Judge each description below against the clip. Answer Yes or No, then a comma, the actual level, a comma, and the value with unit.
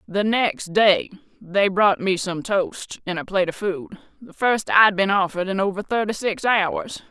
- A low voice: No, high, 195 Hz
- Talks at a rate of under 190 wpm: No, fast, 205 wpm